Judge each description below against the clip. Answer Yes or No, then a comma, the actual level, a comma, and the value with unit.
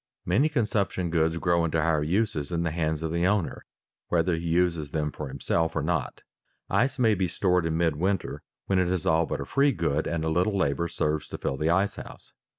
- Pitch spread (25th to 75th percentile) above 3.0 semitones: No, average, 2.7 semitones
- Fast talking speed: Yes, fast, 220 wpm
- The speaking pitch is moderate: No, very low, 85 Hz